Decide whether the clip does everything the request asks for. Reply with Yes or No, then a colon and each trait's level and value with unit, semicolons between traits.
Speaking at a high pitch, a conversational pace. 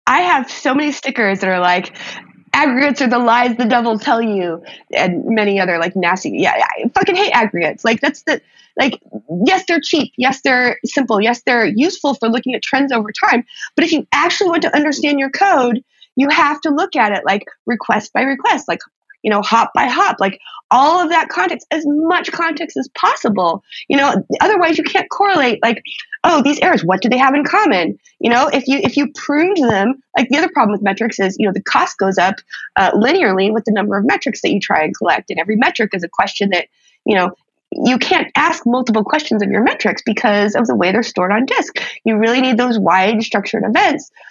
No: very high, 255 Hz; fast, 220 wpm